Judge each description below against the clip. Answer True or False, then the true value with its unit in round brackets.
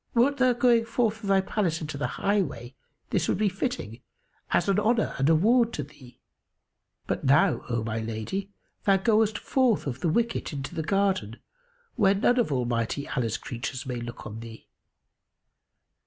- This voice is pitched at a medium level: True (180 Hz)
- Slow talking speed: False (170 wpm)